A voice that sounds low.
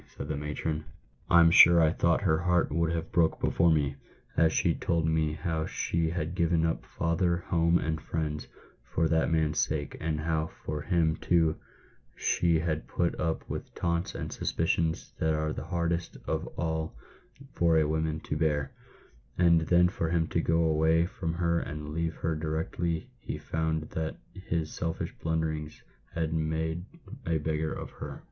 Yes: very low, 80 Hz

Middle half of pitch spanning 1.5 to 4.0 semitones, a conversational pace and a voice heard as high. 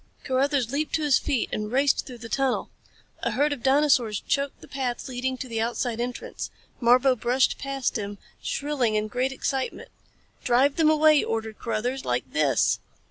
Yes: average, 3.1 semitones; average, 170 wpm; very high, 255 Hz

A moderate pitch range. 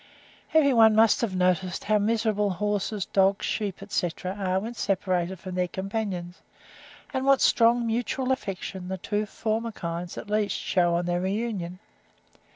Yes: average, 3.3 semitones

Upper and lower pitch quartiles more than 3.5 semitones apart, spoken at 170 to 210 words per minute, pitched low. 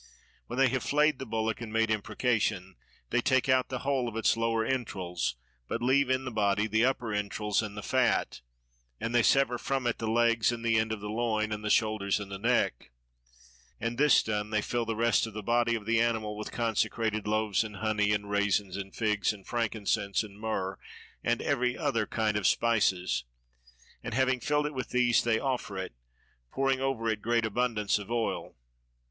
No: narrow, 2.5 semitones; average, 200 wpm; low, 110 Hz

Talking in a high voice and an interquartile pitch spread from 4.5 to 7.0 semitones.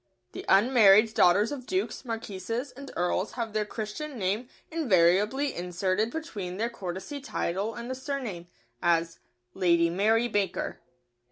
Yes: high, 215 Hz; average, 5.2 semitones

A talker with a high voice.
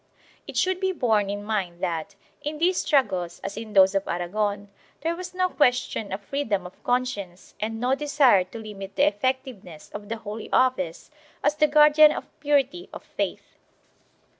Yes: high, 225 Hz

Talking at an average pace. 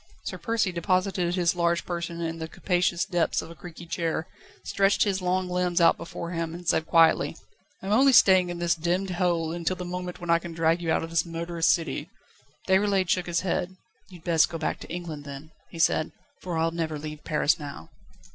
No: fast, 210 wpm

